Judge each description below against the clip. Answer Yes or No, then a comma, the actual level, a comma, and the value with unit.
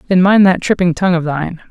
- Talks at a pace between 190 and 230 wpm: No, fast, 245 wpm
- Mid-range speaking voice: Yes, medium, 180 Hz